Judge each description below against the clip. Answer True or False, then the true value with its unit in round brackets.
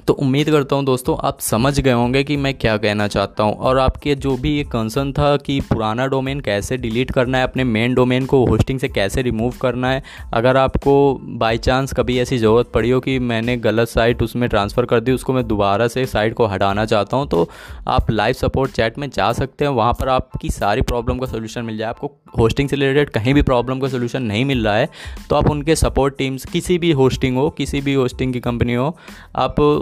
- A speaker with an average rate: False (225 wpm)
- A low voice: True (130 Hz)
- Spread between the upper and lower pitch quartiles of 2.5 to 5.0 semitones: True (2.8 semitones)